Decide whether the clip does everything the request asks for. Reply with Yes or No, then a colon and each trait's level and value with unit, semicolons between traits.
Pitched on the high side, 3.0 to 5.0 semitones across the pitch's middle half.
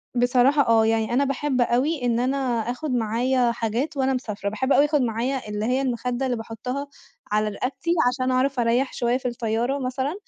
No: very high, 250 Hz; narrow, 2.6 semitones